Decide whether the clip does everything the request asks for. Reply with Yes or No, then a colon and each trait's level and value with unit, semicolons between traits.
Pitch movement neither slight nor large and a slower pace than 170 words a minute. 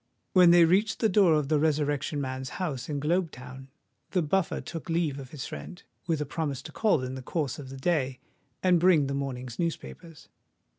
No: average, 4.2 semitones; average, 200 wpm